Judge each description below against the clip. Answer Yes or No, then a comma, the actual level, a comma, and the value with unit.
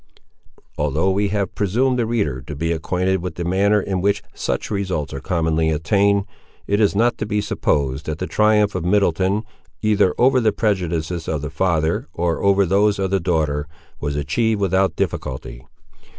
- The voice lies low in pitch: Yes, very low, 95 Hz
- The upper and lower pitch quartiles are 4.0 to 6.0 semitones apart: Yes, average, 4.3 semitones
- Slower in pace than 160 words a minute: No, average, 175 wpm